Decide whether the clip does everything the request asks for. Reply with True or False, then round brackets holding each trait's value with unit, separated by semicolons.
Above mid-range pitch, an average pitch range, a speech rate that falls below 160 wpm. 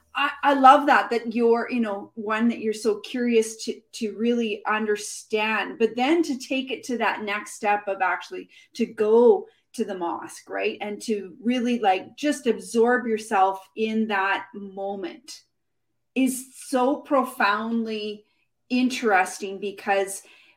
True (225 Hz; 3.6 semitones; 140 wpm)